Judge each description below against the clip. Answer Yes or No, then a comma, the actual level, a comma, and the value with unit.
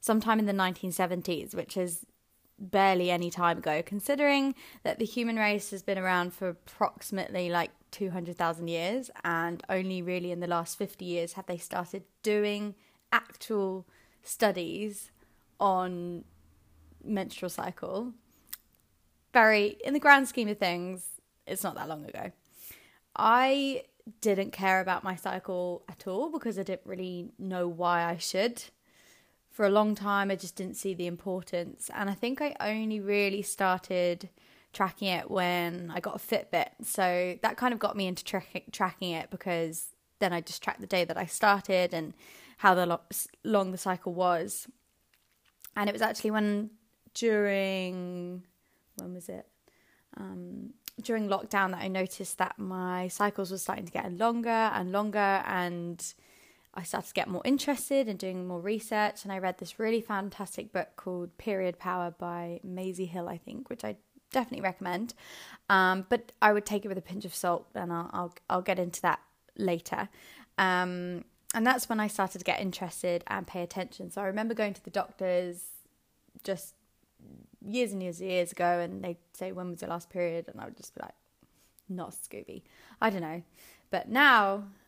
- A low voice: No, high, 190 Hz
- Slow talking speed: No, average, 170 wpm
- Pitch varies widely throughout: No, average, 3.0 semitones